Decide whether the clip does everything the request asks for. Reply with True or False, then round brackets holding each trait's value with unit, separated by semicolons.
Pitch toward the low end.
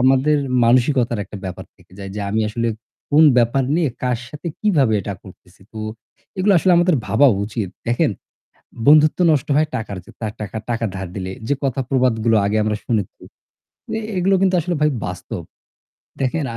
True (120 Hz)